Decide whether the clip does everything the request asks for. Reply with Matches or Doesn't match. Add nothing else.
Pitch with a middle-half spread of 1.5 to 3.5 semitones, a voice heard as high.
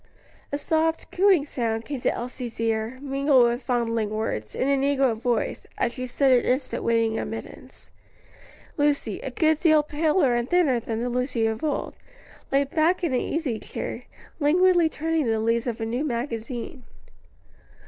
Doesn't match